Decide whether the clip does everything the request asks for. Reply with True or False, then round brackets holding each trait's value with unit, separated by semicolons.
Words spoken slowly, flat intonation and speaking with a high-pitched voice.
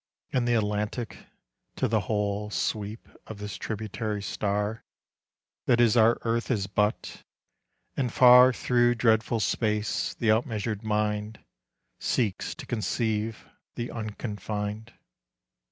False (115 wpm; 2.0 semitones; 110 Hz)